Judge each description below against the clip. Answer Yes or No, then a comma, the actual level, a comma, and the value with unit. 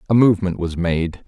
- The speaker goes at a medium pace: Yes, average, 190 wpm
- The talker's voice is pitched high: No, very low, 90 Hz